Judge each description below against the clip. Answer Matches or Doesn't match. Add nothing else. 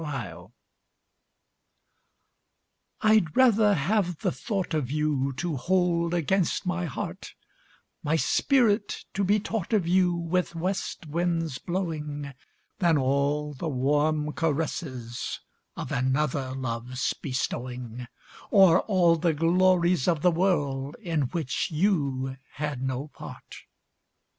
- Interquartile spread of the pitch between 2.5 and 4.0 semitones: Doesn't match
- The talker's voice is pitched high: Doesn't match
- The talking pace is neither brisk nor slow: Doesn't match